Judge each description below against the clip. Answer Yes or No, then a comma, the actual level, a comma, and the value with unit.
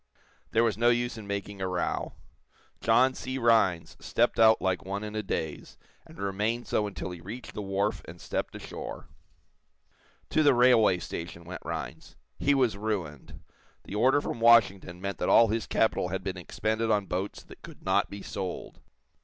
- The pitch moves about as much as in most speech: Yes, average, 3.5 semitones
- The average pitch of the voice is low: Yes, low, 105 Hz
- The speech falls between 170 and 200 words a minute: Yes, average, 180 wpm